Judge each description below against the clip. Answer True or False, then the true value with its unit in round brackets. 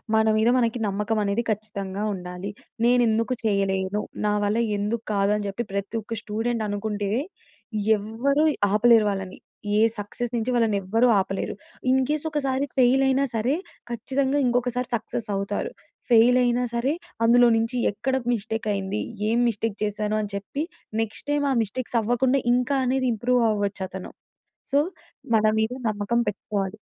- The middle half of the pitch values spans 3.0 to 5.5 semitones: True (3.3 semitones)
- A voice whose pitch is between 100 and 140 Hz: False (225 Hz)